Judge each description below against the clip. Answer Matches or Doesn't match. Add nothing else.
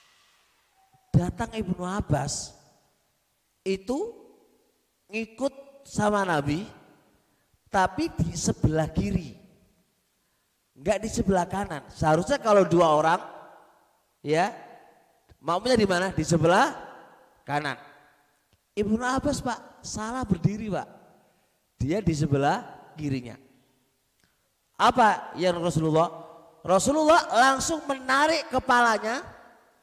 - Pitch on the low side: Doesn't match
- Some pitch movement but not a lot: Doesn't match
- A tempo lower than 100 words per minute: Matches